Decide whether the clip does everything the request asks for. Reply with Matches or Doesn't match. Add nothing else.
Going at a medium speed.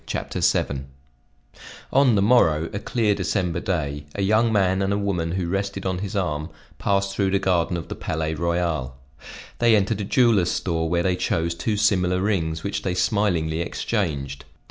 Matches